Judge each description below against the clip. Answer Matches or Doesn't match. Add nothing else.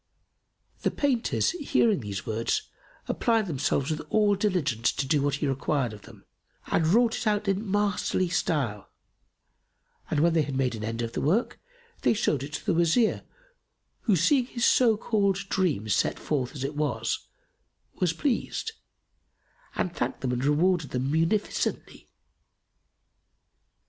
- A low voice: Doesn't match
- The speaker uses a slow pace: Doesn't match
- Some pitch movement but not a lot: Doesn't match